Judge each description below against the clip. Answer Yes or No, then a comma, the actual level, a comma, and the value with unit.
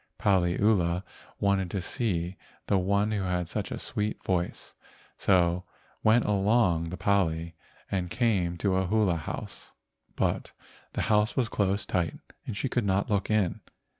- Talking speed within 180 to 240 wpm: No, average, 150 wpm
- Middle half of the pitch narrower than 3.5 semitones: Yes, average, 2.9 semitones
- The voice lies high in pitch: No, very low, 95 Hz